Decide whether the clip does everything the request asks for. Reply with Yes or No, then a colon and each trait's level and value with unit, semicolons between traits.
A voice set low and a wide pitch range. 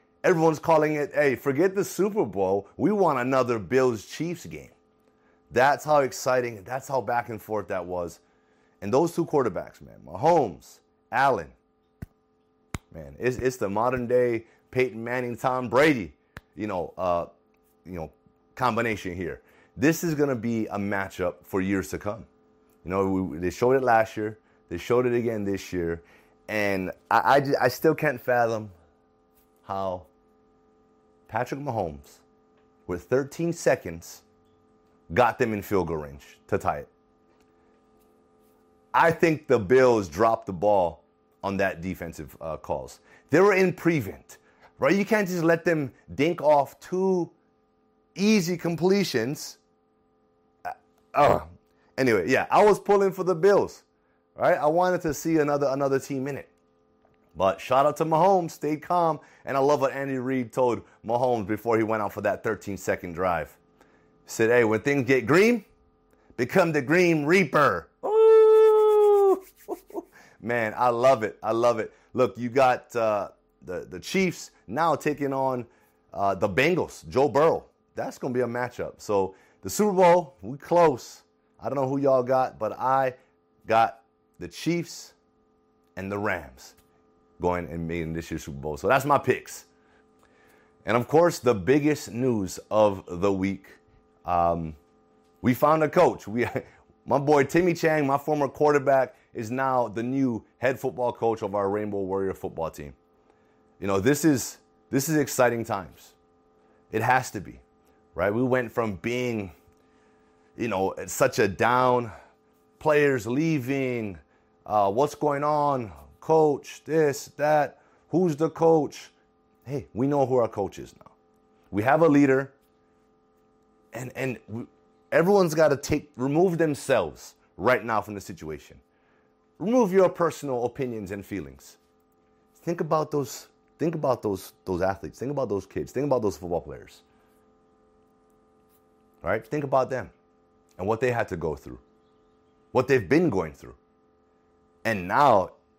Yes: low, 110 Hz; wide, 8.3 semitones